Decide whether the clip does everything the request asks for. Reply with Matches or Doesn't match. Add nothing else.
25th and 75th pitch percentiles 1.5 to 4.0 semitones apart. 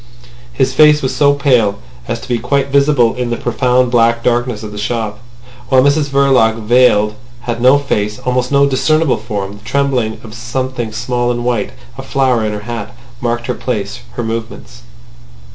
Matches